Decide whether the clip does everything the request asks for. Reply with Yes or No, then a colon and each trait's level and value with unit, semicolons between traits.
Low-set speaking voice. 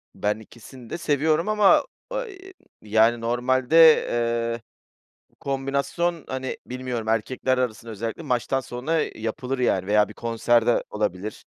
Yes: low, 120 Hz